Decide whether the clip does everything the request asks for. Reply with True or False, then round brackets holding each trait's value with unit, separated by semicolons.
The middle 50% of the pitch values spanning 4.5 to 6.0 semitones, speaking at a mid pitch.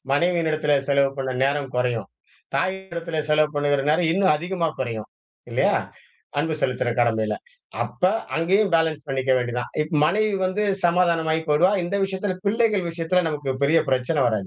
True (4.8 semitones; 160 Hz)